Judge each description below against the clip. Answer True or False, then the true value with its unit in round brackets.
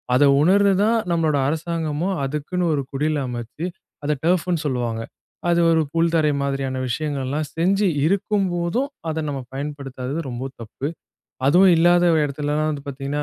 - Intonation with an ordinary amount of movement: True (3.9 semitones)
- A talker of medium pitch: True (155 Hz)